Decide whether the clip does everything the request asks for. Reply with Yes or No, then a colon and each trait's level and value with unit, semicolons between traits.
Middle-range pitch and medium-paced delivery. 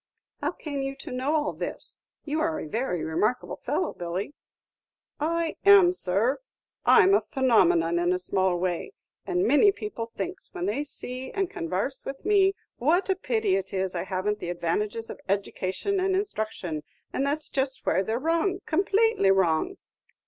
No: very high, 260 Hz; average, 170 wpm